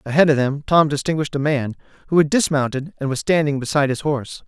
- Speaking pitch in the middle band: Yes, medium, 145 Hz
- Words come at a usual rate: No, fast, 215 wpm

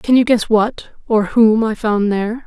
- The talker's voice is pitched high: Yes, high, 220 Hz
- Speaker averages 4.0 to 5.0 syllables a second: Yes, 4.4 syllables/s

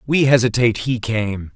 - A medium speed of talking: Yes, average, 155 wpm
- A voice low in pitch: Yes, low, 120 Hz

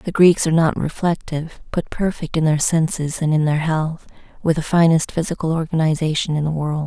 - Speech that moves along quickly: No, average, 190 wpm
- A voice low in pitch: No, medium, 160 Hz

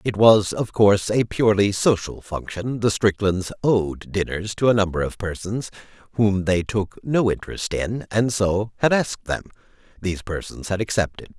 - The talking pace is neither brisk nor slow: Yes, average, 170 wpm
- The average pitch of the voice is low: Yes, low, 100 Hz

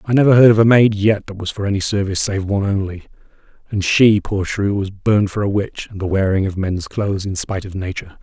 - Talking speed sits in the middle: No, fast, 250 wpm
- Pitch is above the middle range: No, low, 100 Hz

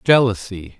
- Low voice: Yes, low, 105 Hz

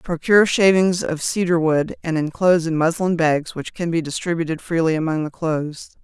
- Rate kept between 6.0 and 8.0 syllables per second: No, 5.4 syllables/s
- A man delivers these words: No, female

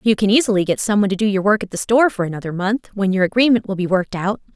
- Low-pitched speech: No, high, 205 Hz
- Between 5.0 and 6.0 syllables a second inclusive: No, 7.5 syllables/s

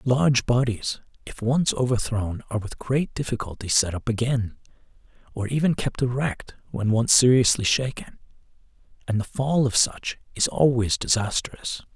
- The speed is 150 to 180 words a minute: No, average, 140 wpm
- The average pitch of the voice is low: Yes, low, 120 Hz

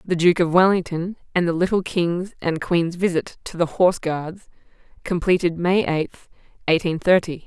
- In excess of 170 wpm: No, average, 160 wpm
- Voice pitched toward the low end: No, medium, 175 Hz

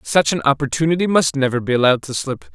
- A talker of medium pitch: Yes, medium, 145 Hz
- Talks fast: Yes, fast, 210 wpm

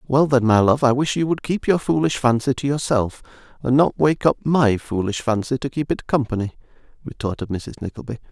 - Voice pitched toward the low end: Yes, low, 130 Hz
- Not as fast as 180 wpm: No, average, 200 wpm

